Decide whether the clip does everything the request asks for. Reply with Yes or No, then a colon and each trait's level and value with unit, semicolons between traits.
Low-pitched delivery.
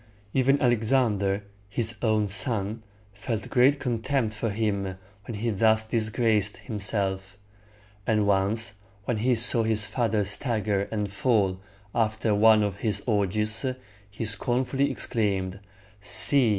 Yes: low, 110 Hz